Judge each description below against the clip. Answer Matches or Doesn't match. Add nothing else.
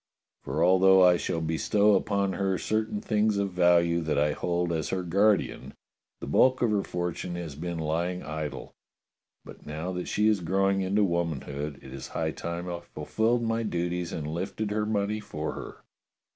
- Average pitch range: Matches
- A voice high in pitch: Doesn't match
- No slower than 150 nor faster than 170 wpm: Doesn't match